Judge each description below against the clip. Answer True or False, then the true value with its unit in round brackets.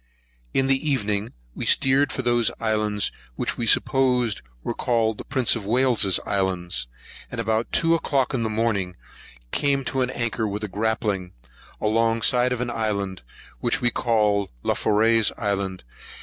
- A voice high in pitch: False (115 Hz)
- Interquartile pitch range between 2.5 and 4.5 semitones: True (3.3 semitones)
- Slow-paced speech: False (155 wpm)